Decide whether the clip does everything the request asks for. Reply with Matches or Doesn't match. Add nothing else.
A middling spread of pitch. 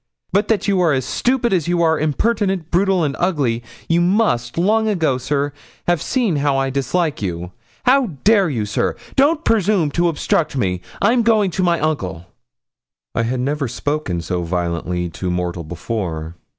Doesn't match